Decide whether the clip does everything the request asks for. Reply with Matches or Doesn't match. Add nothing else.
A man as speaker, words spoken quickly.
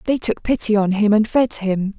Doesn't match